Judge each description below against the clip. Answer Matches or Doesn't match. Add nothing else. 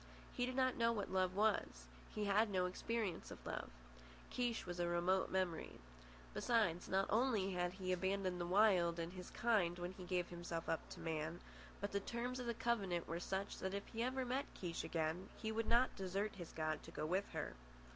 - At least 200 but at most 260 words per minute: Matches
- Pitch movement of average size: Matches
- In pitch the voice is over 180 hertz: Matches